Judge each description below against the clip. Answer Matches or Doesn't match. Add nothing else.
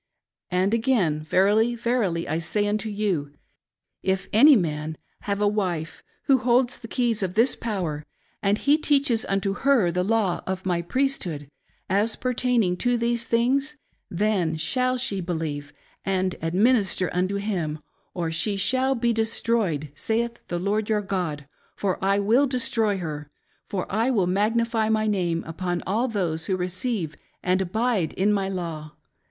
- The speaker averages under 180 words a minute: Matches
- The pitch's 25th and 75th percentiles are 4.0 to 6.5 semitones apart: Matches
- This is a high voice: Matches